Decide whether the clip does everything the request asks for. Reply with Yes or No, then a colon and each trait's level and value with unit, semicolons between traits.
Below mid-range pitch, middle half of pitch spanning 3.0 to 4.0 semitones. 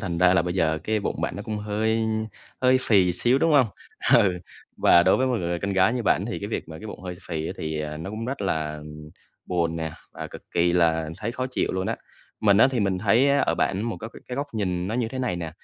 No: very low, 95 Hz; average, 4.9 semitones